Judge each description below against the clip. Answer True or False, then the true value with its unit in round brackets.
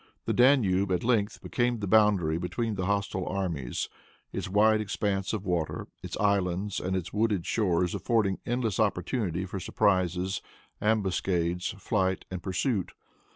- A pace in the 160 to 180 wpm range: False (140 wpm)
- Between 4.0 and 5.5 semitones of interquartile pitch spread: False (2.9 semitones)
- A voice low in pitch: True (95 Hz)